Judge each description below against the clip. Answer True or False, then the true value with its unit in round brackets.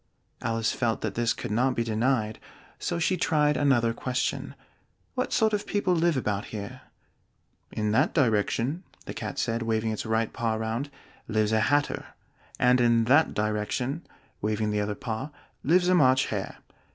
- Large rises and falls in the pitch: False (4.7 semitones)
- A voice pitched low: True (115 Hz)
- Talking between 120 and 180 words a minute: True (165 wpm)